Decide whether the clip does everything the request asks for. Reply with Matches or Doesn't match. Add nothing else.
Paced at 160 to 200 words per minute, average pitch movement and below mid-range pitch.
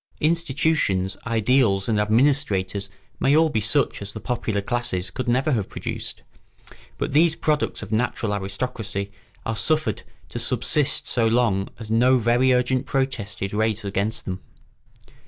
Doesn't match